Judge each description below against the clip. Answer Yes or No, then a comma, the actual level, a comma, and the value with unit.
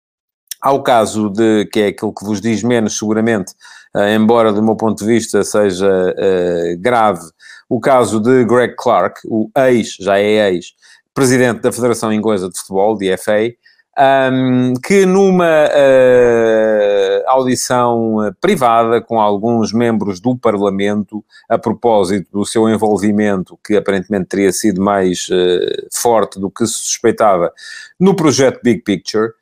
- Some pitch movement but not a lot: Yes, average, 3.1 semitones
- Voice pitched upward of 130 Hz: No, low, 110 Hz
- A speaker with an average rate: Yes, average, 145 wpm